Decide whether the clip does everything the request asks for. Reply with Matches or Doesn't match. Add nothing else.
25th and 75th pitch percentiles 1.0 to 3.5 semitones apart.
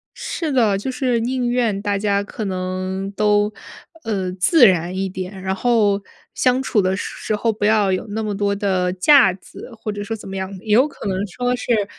Matches